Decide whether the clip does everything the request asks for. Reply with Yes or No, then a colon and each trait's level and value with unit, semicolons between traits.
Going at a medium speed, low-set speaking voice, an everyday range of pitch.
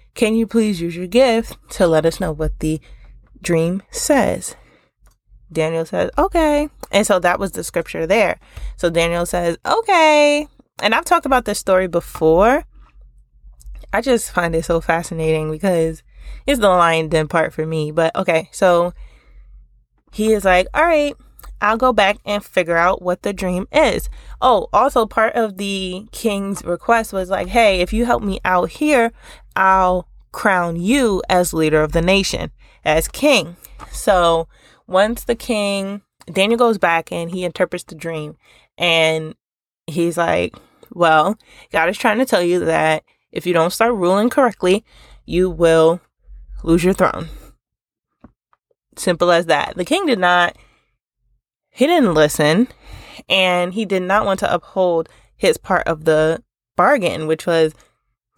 No: average, 155 wpm; medium, 180 Hz; average, 4.9 semitones